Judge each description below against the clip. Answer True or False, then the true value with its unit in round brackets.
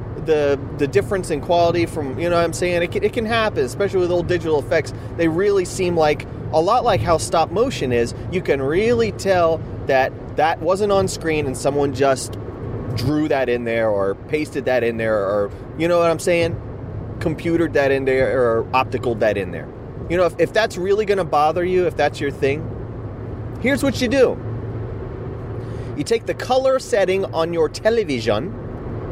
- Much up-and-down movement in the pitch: True (6.1 semitones)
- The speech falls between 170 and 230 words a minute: True (195 wpm)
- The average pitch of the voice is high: False (145 Hz)